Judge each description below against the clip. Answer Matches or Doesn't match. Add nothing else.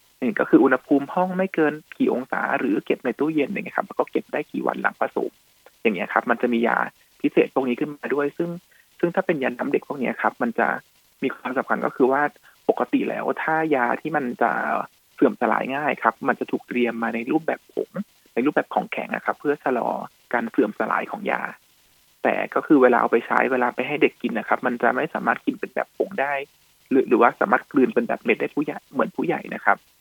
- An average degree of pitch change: Matches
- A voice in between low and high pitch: Matches